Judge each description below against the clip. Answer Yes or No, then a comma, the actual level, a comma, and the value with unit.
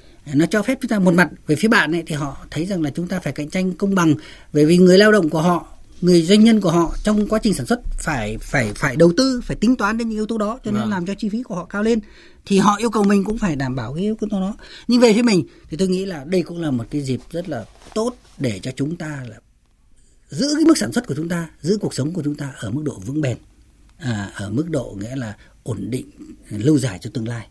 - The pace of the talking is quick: Yes, fast, 285 wpm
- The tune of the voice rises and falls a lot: Yes, wide, 6.8 semitones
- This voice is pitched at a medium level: Yes, medium, 170 Hz